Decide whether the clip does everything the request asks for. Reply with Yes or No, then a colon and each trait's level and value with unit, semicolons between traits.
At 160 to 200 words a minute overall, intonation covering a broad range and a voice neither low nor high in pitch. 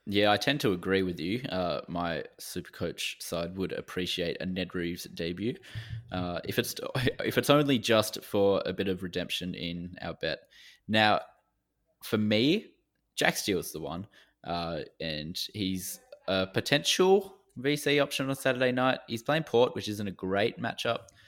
No: average, 165 wpm; wide, 6.0 semitones; low, 100 Hz